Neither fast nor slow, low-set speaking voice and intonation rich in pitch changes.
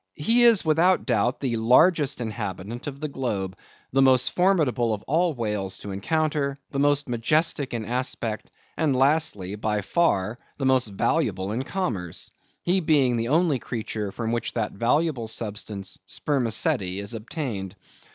Yes: average, 150 wpm; low, 125 Hz; wide, 6.1 semitones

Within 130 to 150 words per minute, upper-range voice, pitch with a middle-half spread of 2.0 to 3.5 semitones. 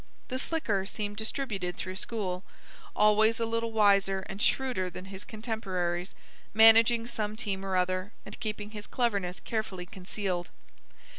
Yes: average, 140 wpm; high, 205 Hz; average, 3.1 semitones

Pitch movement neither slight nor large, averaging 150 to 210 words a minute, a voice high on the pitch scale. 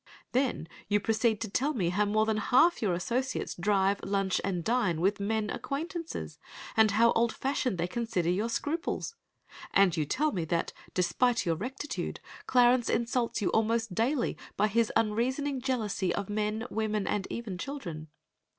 Yes: average, 4.0 semitones; average, 160 wpm; high, 220 Hz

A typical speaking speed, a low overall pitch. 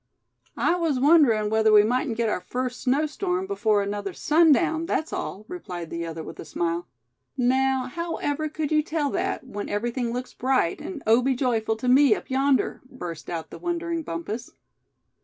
No: average, 175 wpm; very high, 255 Hz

